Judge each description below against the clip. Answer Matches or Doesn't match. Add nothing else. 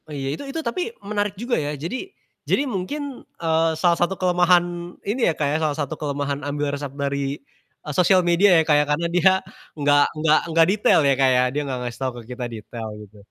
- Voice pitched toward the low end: Doesn't match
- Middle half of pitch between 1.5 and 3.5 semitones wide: Doesn't match